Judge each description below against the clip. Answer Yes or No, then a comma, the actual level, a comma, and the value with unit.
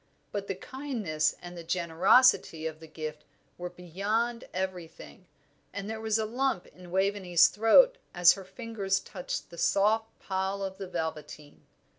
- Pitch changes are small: No, average, 4.2 semitones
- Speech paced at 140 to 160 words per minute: Yes, average, 150 wpm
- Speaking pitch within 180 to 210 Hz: Yes, high, 190 Hz